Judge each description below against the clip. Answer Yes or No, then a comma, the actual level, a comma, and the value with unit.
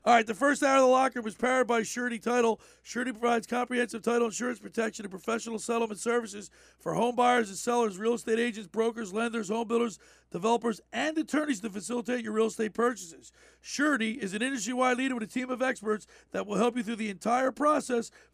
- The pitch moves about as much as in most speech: No, narrow, 1.7 semitones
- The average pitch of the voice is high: Yes, high, 235 Hz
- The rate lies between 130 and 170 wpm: No, fast, 205 wpm